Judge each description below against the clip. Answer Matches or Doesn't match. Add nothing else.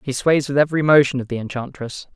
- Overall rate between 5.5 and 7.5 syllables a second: Matches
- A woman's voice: Doesn't match